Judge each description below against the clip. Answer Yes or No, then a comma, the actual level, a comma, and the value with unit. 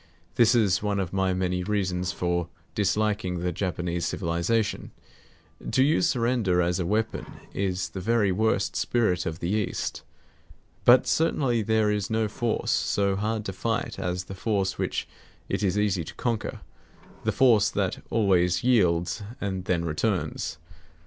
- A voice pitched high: No, low, 100 Hz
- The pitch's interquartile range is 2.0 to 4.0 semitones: Yes, average, 3.6 semitones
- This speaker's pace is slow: No, average, 150 wpm